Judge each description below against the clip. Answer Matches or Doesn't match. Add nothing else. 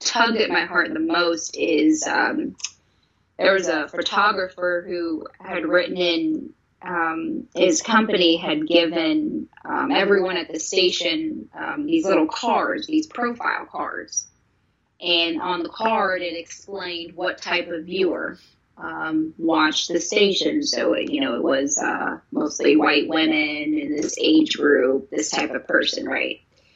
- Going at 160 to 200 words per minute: Doesn't match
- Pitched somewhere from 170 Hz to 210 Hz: Matches